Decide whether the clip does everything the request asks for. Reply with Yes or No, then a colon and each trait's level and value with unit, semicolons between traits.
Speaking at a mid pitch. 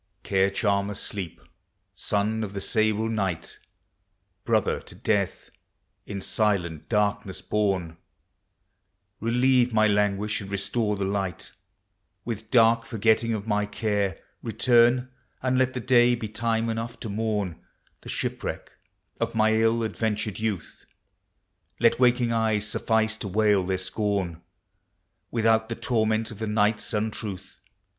No: low, 110 Hz